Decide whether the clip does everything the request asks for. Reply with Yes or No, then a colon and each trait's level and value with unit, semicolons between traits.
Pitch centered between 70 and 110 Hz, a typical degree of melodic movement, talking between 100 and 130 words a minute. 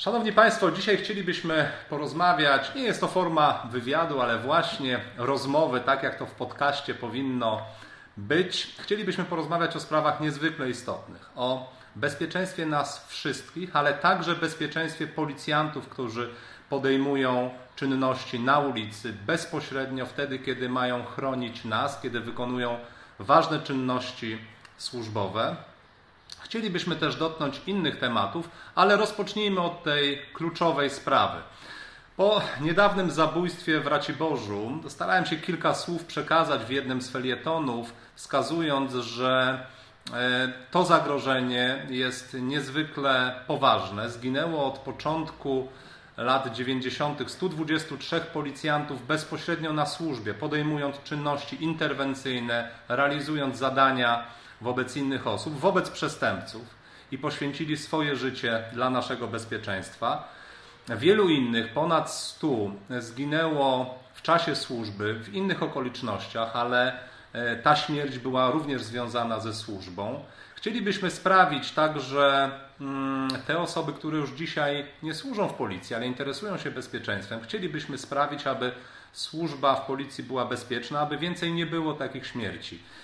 No: medium, 140 Hz; average, 3.9 semitones; average, 115 wpm